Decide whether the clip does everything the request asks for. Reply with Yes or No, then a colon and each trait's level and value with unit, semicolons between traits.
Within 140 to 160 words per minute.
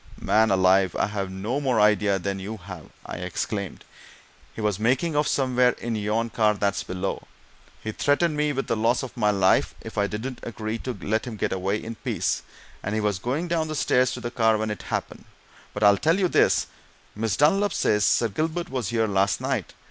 No: fast, 205 wpm